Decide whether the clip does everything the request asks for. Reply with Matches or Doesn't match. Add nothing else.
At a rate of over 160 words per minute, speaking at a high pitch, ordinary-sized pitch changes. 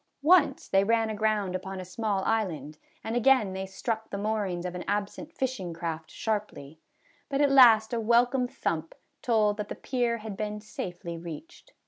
Matches